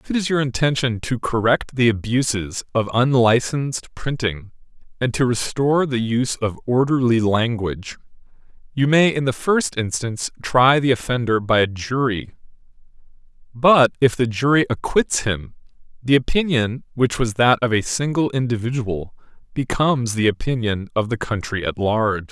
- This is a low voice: Yes, low, 120 Hz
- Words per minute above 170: No, average, 150 wpm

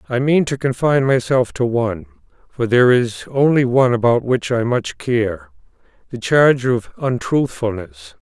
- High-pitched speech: No, low, 125 Hz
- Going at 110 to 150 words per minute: Yes, average, 145 wpm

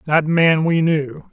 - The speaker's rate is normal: Yes, average, 180 wpm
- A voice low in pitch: No, medium, 155 Hz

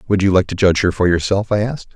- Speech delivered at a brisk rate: Yes, fast, 275 wpm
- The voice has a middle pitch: No, very low, 95 Hz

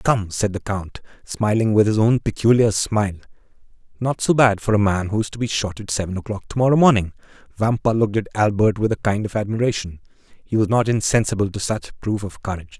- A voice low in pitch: Yes, low, 105 Hz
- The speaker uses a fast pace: Yes, fast, 215 wpm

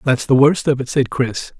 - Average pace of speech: No, fast, 265 wpm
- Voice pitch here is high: No, low, 135 Hz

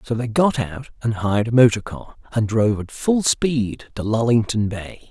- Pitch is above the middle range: No, low, 115 Hz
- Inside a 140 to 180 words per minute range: No, average, 200 wpm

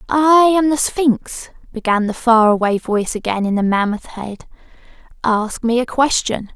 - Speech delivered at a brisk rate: No, average, 165 wpm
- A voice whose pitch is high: Yes, high, 235 Hz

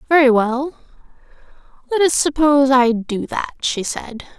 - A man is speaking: No, female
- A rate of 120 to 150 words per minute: Yes, slow, 135 wpm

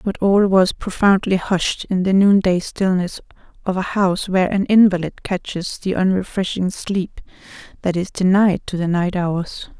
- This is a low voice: No, medium, 185 Hz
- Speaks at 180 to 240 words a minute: No, average, 160 wpm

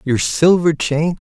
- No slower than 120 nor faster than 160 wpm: Yes, average, 140 wpm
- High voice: No, medium, 160 Hz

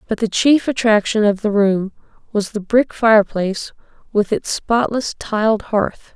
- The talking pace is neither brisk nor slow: Yes, average, 155 wpm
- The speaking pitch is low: No, high, 215 Hz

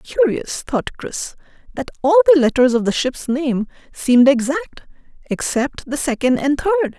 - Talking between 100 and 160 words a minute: Yes, average, 155 wpm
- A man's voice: No, female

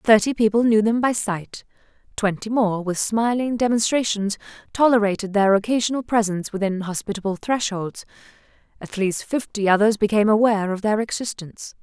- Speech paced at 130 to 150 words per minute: Yes, slow, 135 wpm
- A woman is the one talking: Yes, female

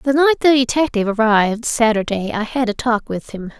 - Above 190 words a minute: Yes, average, 200 wpm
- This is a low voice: No, high, 235 Hz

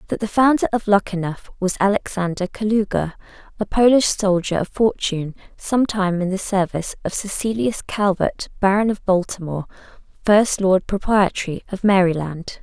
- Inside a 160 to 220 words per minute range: No, average, 140 wpm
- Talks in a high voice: Yes, high, 195 Hz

